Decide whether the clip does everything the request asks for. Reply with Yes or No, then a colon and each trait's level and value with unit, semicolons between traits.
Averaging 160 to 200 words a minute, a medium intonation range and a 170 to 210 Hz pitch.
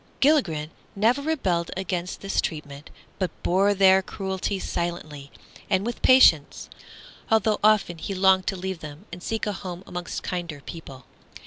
No: average, 145 wpm; average, 3.0 semitones; medium, 185 Hz